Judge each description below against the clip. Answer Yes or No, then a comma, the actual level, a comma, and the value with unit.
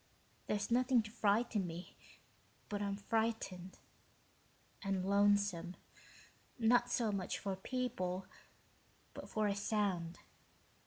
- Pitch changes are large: No, average, 3.0 semitones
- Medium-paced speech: No, slow, 110 wpm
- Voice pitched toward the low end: No, high, 205 Hz